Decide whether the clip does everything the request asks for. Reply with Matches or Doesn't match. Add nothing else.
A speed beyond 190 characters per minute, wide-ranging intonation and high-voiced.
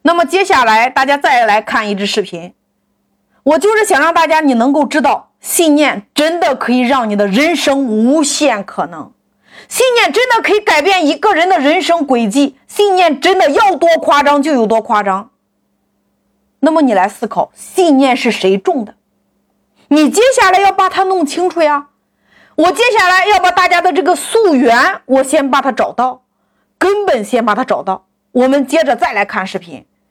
Matches